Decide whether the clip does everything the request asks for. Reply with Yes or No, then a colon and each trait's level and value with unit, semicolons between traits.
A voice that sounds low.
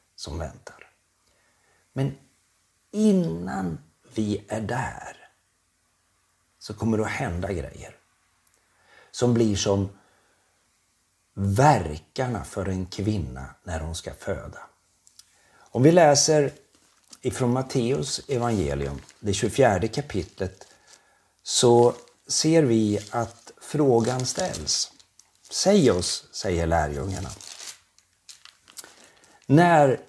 Yes: low, 100 Hz